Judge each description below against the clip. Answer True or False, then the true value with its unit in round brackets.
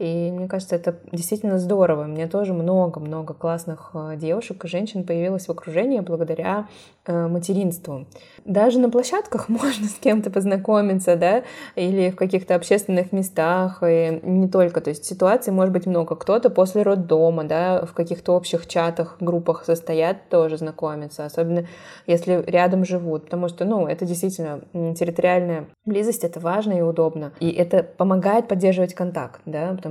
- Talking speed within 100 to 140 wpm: False (150 wpm)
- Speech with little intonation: True (2.2 semitones)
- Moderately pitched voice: True (175 Hz)